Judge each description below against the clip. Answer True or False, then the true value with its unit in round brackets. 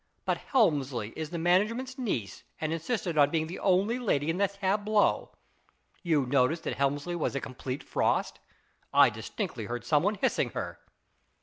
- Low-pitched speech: False (165 Hz)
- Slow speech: False (165 wpm)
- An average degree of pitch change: False (6.2 semitones)